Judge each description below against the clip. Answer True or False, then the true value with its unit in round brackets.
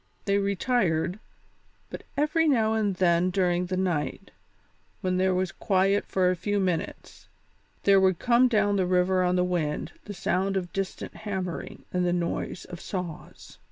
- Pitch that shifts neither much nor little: False (2.0 semitones)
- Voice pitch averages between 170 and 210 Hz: True (185 Hz)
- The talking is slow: False (160 wpm)